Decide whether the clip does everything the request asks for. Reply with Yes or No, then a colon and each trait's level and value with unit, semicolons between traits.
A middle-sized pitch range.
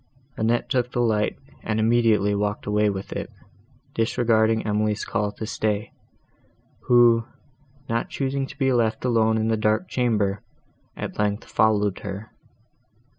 No: narrow, 2.1 semitones